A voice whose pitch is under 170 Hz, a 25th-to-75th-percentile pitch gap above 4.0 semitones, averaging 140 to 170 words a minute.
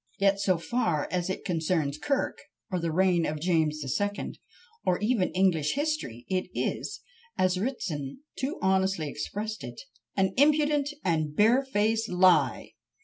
No: medium, 185 Hz; average, 5.2 semitones; average, 150 wpm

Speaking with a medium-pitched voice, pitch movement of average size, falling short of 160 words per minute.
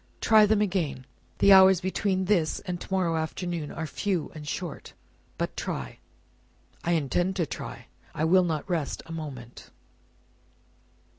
Yes: medium, 175 Hz; average, 3.3 semitones; average, 145 wpm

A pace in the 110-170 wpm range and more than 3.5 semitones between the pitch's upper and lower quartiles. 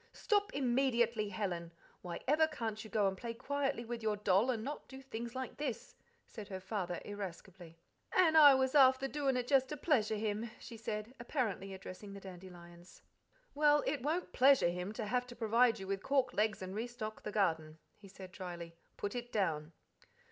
No: average, 190 wpm; wide, 5.4 semitones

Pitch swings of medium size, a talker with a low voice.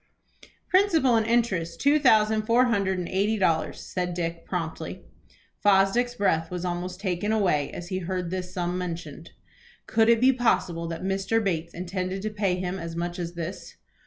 No: average, 3.9 semitones; medium, 185 Hz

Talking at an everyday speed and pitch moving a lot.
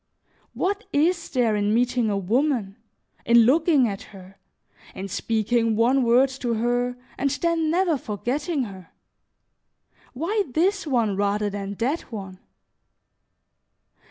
No: slow, 125 wpm; wide, 5.9 semitones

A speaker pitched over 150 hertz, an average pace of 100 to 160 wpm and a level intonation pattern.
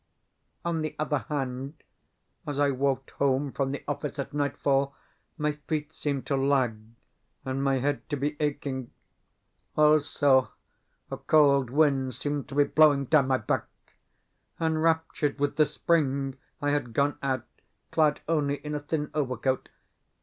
No: medium, 140 Hz; average, 145 wpm; narrow, 1.8 semitones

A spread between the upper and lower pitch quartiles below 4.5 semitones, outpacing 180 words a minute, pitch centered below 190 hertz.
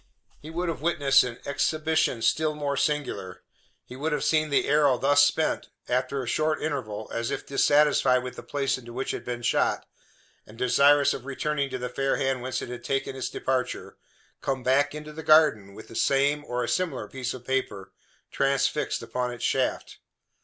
Yes: average, 2.9 semitones; average, 190 wpm; low, 135 Hz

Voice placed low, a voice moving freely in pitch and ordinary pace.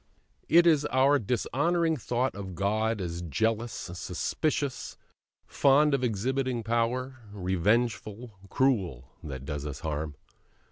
No: low, 115 Hz; wide, 6.2 semitones; slow, 110 wpm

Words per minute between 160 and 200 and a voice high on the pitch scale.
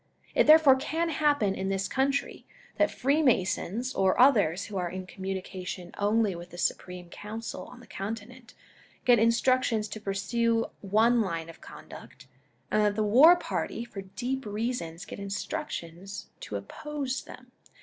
No: average, 150 wpm; high, 215 Hz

